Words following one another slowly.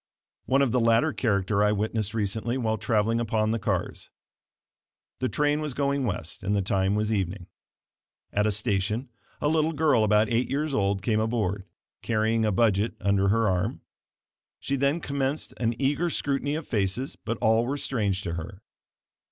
No: average, 170 wpm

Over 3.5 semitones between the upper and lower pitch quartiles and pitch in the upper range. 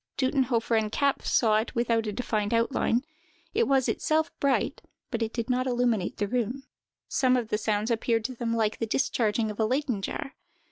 No: average, 2.8 semitones; high, 235 Hz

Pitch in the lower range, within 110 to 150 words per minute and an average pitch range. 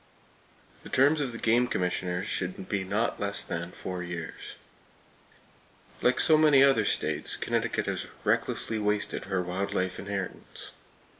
Yes: low, 100 Hz; average, 140 wpm; average, 5.0 semitones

